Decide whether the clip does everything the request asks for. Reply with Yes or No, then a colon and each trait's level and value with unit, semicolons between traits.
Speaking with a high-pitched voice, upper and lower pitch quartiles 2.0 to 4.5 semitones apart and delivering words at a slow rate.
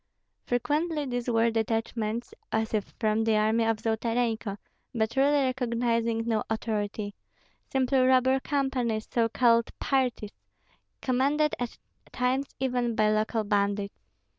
Yes: high, 230 Hz; average, 2.7 semitones; slow, 120 wpm